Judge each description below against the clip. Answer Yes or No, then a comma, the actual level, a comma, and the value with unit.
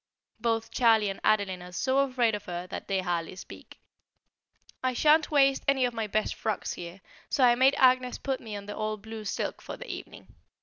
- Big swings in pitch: No, average, 4.4 semitones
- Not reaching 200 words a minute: No, fast, 205 wpm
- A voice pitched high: Yes, high, 225 Hz